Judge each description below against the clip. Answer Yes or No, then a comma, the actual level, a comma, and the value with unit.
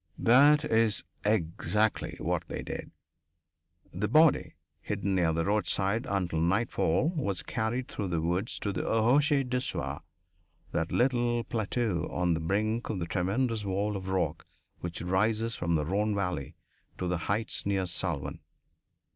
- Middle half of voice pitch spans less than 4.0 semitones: No, average, 4.5 semitones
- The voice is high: No, low, 100 Hz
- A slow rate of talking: No, average, 145 wpm